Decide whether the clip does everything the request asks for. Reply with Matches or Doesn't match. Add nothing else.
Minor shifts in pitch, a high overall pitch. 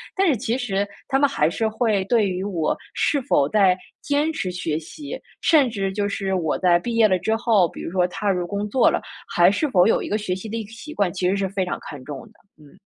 Doesn't match